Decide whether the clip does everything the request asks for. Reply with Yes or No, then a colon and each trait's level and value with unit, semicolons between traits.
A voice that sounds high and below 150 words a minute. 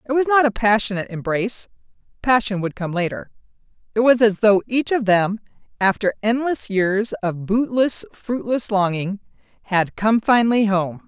Yes: high, 215 Hz; average, 140 wpm